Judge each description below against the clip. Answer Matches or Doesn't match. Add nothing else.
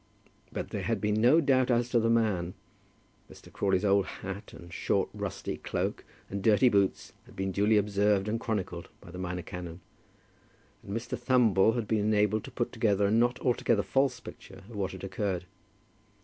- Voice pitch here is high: Doesn't match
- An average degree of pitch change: Matches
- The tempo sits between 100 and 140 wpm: Doesn't match